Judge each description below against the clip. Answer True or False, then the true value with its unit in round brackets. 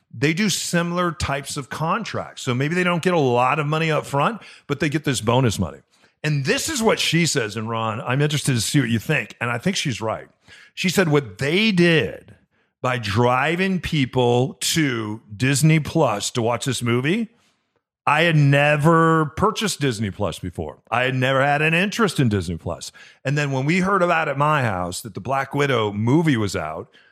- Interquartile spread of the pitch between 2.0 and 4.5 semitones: False (5.6 semitones)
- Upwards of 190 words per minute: True (200 wpm)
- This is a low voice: False (145 Hz)